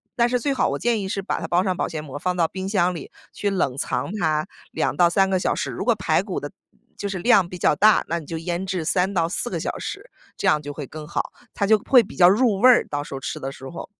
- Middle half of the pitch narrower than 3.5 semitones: No, average, 4.1 semitones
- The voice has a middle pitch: Yes, medium, 180 Hz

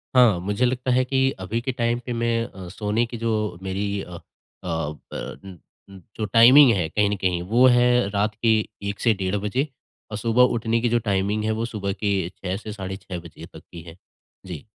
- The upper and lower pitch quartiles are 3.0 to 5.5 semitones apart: Yes, average, 3.7 semitones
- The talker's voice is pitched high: No, low, 105 Hz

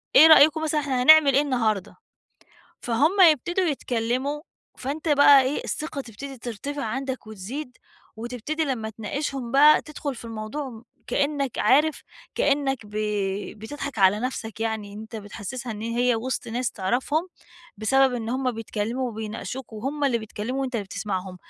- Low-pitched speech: No, very high, 255 Hz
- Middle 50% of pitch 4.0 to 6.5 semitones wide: Yes, average, 4.3 semitones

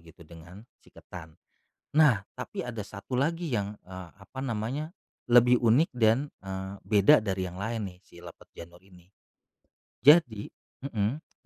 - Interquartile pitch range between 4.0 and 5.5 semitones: Yes, average, 5.0 semitones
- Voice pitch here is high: No, low, 105 Hz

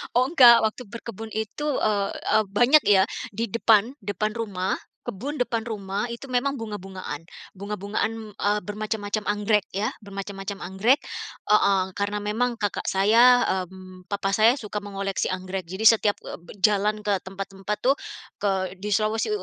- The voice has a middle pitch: No, high, 210 Hz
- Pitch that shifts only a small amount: Yes, narrow, 2.3 semitones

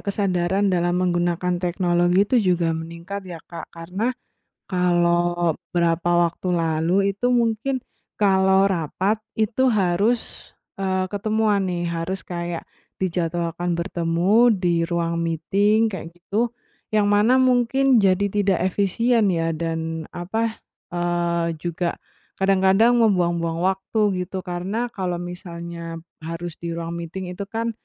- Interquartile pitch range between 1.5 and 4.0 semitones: Yes, average, 2.9 semitones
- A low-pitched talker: No, medium, 180 Hz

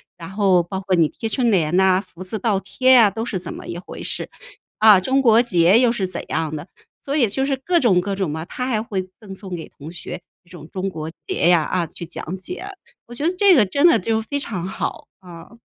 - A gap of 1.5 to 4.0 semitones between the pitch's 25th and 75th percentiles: No, average, 4.9 semitones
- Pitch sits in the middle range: No, high, 195 Hz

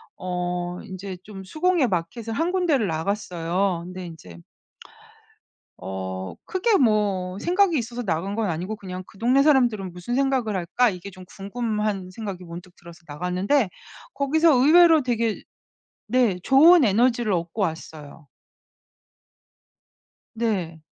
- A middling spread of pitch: No, wide, 5.7 semitones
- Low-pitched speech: No, high, 200 Hz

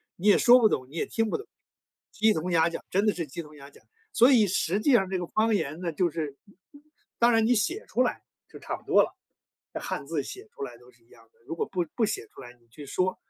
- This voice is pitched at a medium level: Yes, medium, 180 Hz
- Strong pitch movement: Yes, wide, 6.9 semitones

